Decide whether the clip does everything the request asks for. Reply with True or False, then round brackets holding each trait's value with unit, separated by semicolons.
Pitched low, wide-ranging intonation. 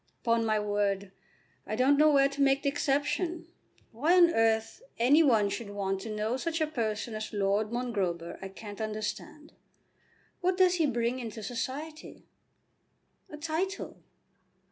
False (240 Hz; 5.9 semitones)